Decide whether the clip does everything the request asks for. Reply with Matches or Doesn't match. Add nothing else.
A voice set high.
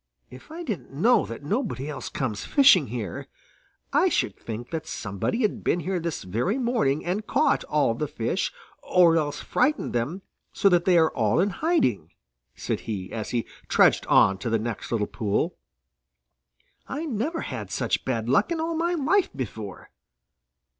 Doesn't match